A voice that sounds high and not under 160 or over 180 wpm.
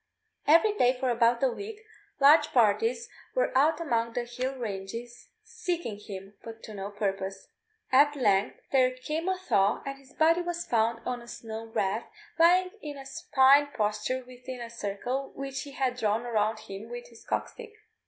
Yes: very high, 250 Hz; average, 175 wpm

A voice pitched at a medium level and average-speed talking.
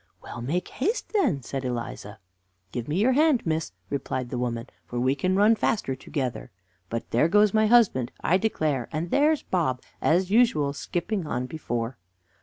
Yes: medium, 155 Hz; average, 170 wpm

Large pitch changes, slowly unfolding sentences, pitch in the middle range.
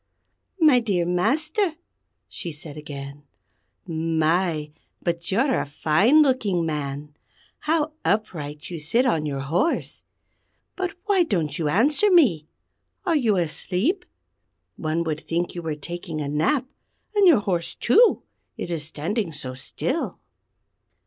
Yes: wide, 9.0 semitones; slow, 130 wpm; medium, 175 Hz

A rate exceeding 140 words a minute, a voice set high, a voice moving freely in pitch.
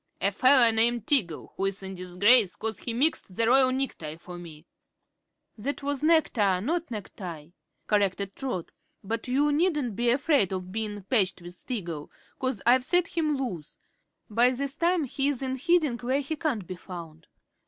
Yes: average, 165 wpm; high, 230 Hz; wide, 6.5 semitones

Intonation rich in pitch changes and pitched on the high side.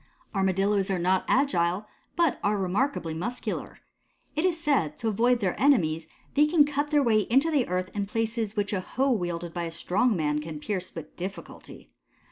Yes: wide, 6.6 semitones; high, 205 Hz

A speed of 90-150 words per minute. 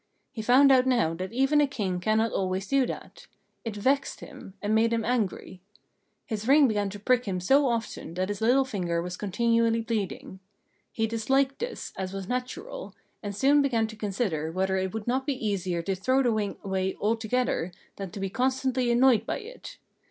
No: average, 190 wpm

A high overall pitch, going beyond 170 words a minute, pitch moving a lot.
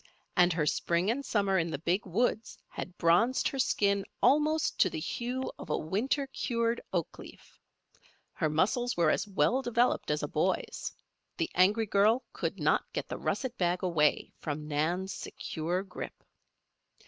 No: high, 195 Hz; average, 160 wpm; wide, 5.9 semitones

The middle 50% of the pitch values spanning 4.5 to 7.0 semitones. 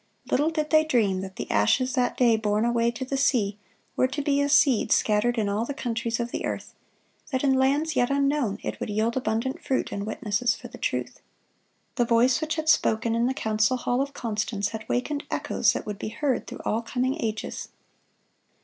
No: average, 3.9 semitones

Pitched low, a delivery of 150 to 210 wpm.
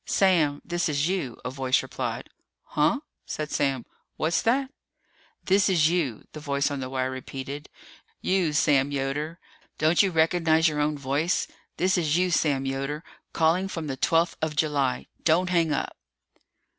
No: medium, 155 Hz; average, 155 wpm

